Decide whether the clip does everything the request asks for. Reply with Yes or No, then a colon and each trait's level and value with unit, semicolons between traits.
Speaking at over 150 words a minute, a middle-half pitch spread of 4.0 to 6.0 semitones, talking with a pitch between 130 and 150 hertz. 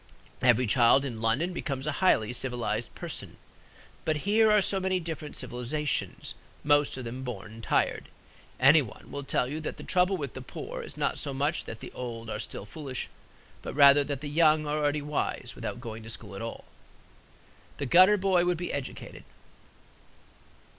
Yes: average, 175 wpm; average, 4.6 semitones; medium, 140 Hz